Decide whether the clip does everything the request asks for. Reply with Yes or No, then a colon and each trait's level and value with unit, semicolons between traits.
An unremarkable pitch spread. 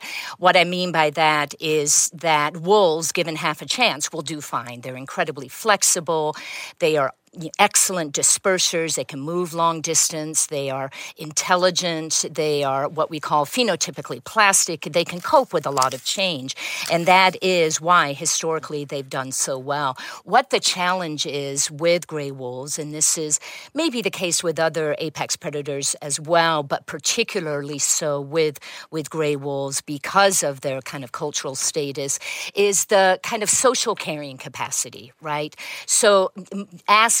Yes: average, 3.8 semitones